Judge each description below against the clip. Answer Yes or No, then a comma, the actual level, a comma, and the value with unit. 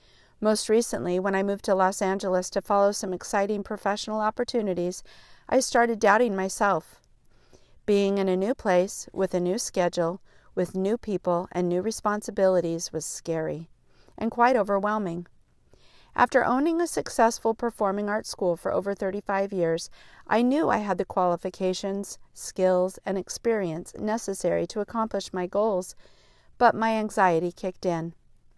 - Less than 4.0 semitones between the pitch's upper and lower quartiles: Yes, average, 2.9 semitones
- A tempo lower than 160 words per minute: Yes, average, 145 wpm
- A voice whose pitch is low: No, high, 195 Hz